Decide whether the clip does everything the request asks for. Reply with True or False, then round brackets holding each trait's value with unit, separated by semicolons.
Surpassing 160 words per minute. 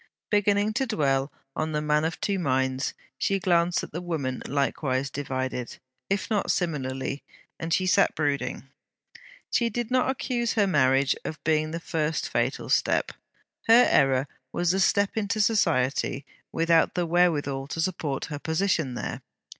False (155 wpm)